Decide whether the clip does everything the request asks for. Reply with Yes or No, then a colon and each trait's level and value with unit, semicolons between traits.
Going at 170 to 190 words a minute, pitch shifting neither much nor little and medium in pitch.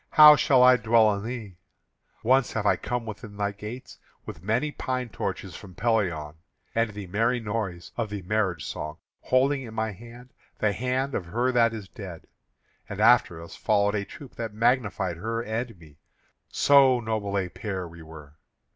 No: average, 175 wpm; average, 3.8 semitones; low, 110 Hz